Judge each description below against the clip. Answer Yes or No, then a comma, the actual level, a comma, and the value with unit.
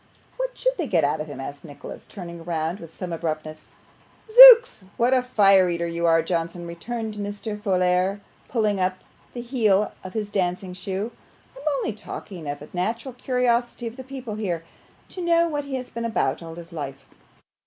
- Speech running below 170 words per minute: No, average, 185 wpm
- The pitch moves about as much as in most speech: No, wide, 6.0 semitones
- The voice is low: No, high, 195 Hz